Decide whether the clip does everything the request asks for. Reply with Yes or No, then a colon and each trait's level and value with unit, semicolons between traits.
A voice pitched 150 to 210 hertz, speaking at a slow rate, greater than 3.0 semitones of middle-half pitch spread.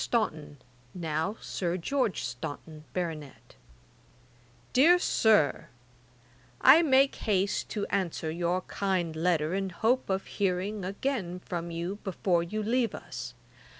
Yes: medium, 185 Hz; slow, 115 wpm; average, 4.2 semitones